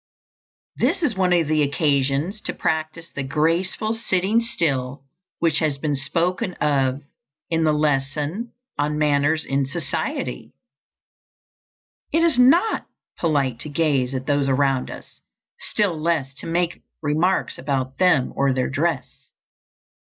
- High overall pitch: No, medium, 150 Hz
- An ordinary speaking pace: No, slow, 130 wpm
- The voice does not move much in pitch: No, average, 4.0 semitones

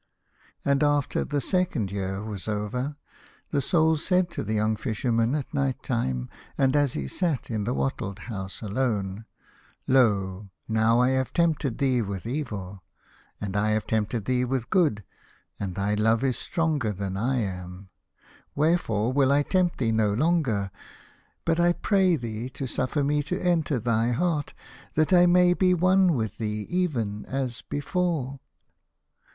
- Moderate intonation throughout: No, wide, 6.1 semitones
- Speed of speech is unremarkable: Yes, average, 160 wpm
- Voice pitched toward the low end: Yes, low, 125 Hz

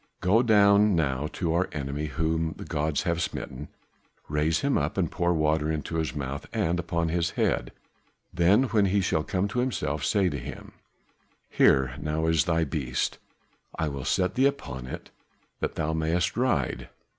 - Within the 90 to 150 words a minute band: No, average, 170 wpm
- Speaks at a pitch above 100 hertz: No, very low, 80 Hz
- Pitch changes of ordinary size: Yes, average, 3.6 semitones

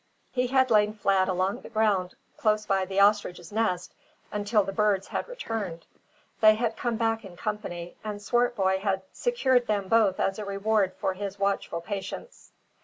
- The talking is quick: No, average, 170 wpm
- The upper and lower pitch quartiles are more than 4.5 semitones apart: No, narrow, 2.6 semitones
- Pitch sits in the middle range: No, high, 205 Hz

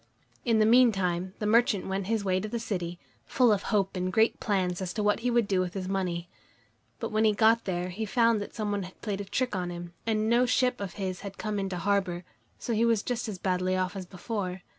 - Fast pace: Yes, fast, 245 wpm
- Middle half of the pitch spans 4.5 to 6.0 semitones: No, average, 3.2 semitones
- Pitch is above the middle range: Yes, high, 200 Hz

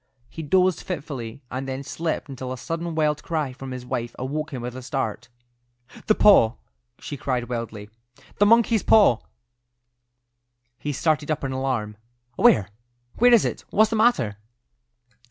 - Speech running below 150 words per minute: No, average, 155 wpm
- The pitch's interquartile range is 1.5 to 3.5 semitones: No, average, 5.0 semitones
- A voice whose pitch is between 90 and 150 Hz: Yes, low, 135 Hz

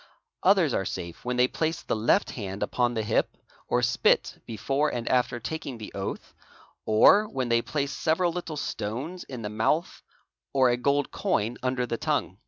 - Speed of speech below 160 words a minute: No, average, 180 wpm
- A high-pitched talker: No, low, 125 Hz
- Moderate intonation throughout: Yes, average, 5.0 semitones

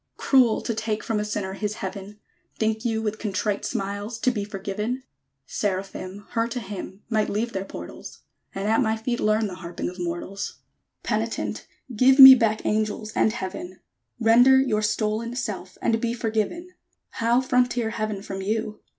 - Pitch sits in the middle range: No, high, 215 Hz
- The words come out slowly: No, average, 165 wpm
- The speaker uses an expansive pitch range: No, narrow, 2.6 semitones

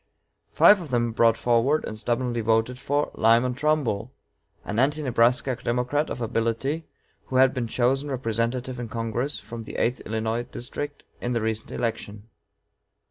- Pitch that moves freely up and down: No, narrow, 2.4 semitones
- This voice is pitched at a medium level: No, low, 120 Hz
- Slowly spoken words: No, average, 150 wpm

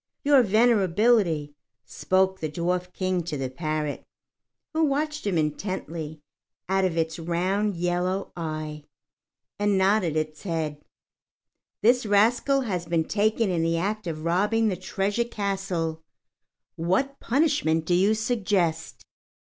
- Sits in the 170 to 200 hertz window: Yes, medium, 185 Hz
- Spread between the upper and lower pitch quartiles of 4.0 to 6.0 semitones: Yes, average, 4.6 semitones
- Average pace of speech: No, slow, 125 wpm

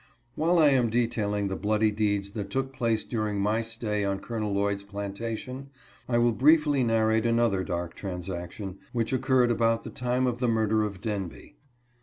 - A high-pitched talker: No, low, 110 Hz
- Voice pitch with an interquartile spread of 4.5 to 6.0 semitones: No, average, 3.0 semitones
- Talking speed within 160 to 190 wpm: Yes, average, 170 wpm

